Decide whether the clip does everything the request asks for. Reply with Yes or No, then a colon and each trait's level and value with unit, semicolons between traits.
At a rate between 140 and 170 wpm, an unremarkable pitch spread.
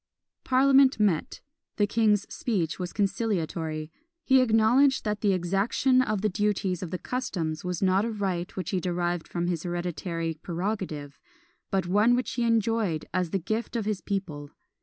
Yes: average, 160 wpm; average, 4.1 semitones